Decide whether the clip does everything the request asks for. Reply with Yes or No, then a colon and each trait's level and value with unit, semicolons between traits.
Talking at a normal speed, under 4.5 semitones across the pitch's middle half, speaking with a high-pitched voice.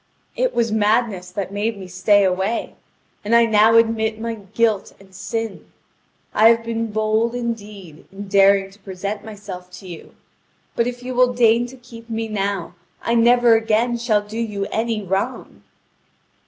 Yes: average, 165 wpm; narrow, 2.6 semitones; high, 220 Hz